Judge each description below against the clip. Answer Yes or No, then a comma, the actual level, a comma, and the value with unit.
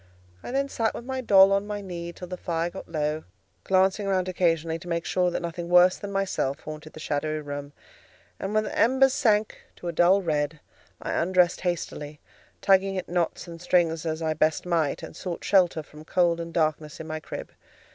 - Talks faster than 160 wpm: Yes, average, 200 wpm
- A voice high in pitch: No, medium, 175 Hz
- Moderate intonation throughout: Yes, average, 3.4 semitones